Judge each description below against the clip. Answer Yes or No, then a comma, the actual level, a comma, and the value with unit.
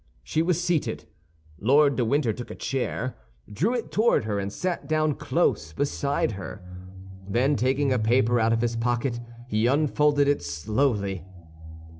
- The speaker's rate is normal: Yes, average, 155 wpm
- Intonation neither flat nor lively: Yes, average, 4.9 semitones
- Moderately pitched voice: No, low, 125 Hz